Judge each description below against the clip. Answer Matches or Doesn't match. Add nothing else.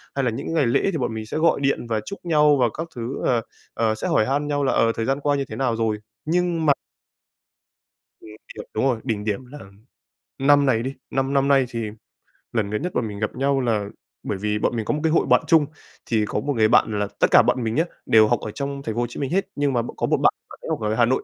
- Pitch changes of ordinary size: Matches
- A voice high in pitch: Doesn't match